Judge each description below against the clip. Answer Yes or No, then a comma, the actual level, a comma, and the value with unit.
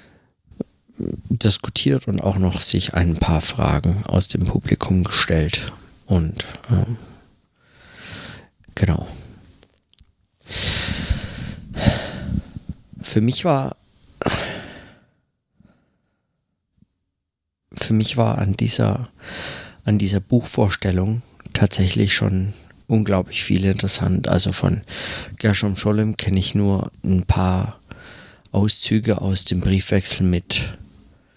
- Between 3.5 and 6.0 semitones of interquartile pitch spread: No, average, 2.9 semitones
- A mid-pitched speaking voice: No, low, 100 Hz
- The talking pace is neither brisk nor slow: No, slow, 85 wpm